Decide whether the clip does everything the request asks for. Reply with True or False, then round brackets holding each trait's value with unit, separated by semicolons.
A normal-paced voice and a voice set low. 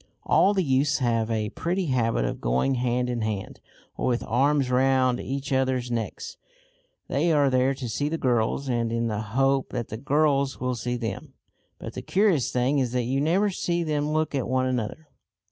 True (195 wpm; 130 Hz)